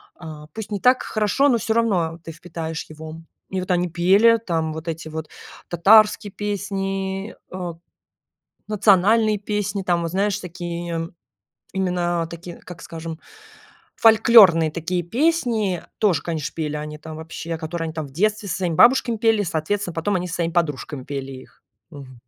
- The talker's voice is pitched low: No, medium, 175 Hz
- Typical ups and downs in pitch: Yes, average, 4.1 semitones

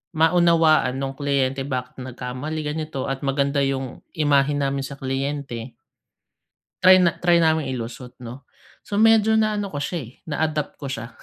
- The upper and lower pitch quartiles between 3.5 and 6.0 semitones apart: No, average, 3.1 semitones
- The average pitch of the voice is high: No, medium, 140 Hz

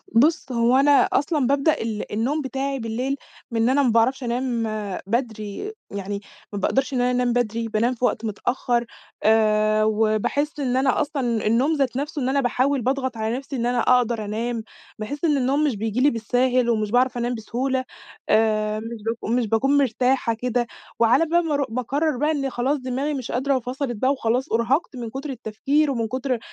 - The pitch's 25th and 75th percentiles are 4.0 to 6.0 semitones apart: No, average, 3.3 semitones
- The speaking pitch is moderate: No, high, 245 Hz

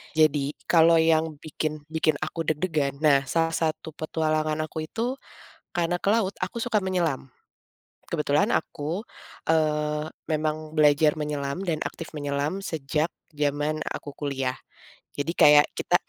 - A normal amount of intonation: No, narrow, 1.8 semitones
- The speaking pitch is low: No, medium, 155 Hz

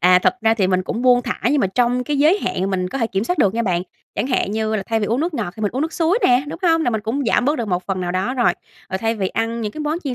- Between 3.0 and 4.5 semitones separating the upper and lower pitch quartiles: No, wide, 5.5 semitones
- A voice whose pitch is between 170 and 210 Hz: No, high, 230 Hz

